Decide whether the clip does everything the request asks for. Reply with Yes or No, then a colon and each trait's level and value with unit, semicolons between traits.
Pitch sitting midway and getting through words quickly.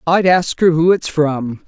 Yes: medium, 160 Hz; fast, 215 wpm